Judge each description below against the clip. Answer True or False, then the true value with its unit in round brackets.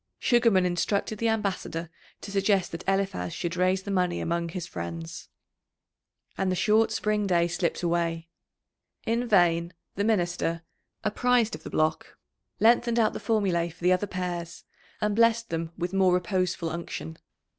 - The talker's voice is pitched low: False (185 Hz)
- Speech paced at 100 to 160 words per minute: True (155 wpm)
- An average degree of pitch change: True (3.7 semitones)